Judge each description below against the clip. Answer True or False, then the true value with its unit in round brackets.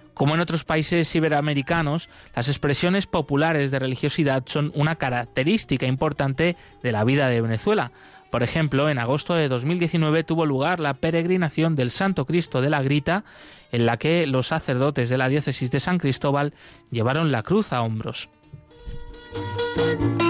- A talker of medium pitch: True (145 Hz)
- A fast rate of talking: False (150 wpm)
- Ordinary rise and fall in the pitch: True (3.9 semitones)